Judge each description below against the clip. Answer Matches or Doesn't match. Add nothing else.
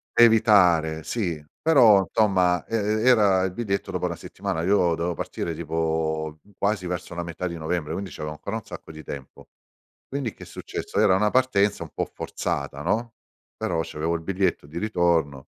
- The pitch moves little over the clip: Doesn't match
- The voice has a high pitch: Doesn't match